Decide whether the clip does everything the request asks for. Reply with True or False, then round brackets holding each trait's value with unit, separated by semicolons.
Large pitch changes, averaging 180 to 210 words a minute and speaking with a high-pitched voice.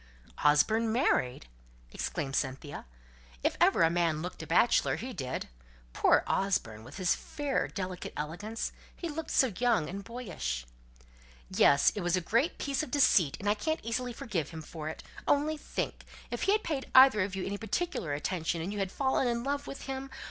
True (8.3 semitones; 185 wpm; 200 Hz)